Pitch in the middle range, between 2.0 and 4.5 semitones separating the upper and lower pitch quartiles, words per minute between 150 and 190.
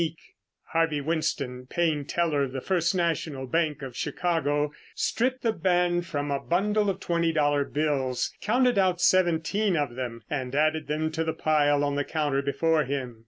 Yes: medium, 155 Hz; average, 3.4 semitones; average, 170 wpm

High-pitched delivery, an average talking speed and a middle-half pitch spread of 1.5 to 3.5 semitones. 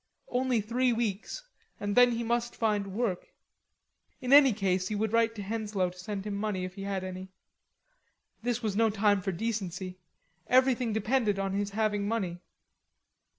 Yes: high, 210 Hz; average, 160 wpm; average, 2.9 semitones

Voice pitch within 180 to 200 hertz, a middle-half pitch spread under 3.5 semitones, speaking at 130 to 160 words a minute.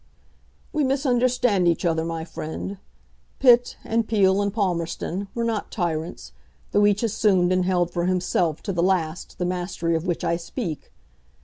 No: medium, 185 Hz; average, 4.0 semitones; average, 155 wpm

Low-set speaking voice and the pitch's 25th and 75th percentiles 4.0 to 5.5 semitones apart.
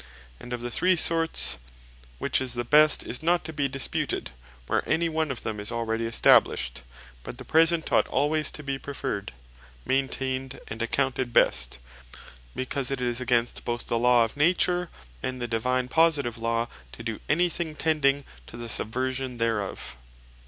Yes: low, 130 Hz; average, 4.4 semitones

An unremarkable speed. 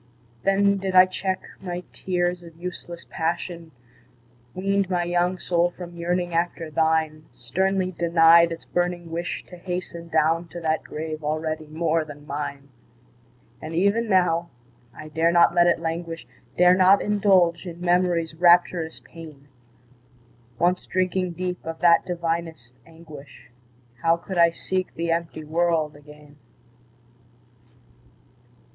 No: slow, 130 wpm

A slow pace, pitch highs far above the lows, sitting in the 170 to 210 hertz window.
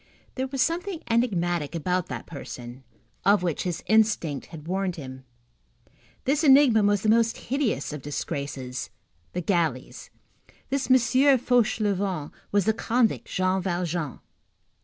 Yes: slow, 130 wpm; wide, 6.5 semitones; high, 190 Hz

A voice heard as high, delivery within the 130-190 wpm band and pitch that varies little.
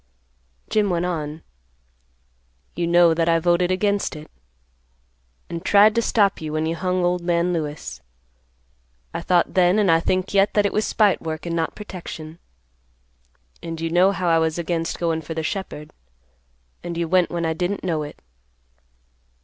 No: medium, 170 Hz; average, 170 wpm; narrow, 2.2 semitones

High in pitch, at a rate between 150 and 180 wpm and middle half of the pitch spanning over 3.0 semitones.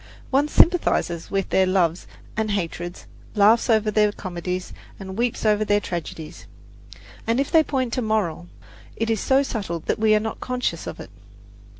Yes: high, 210 Hz; average, 170 wpm; average, 4.1 semitones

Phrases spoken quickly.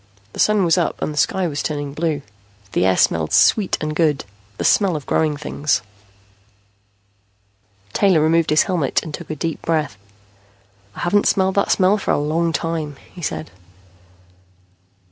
No: average, 165 wpm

